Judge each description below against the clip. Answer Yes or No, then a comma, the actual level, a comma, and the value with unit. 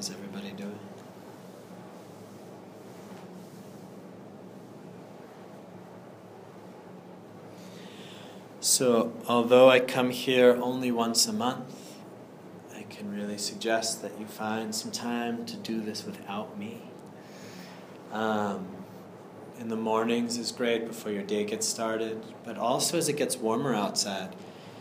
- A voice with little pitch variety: Yes, narrow, 1.9 semitones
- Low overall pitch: Yes, low, 115 Hz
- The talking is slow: Yes, slow, 105 wpm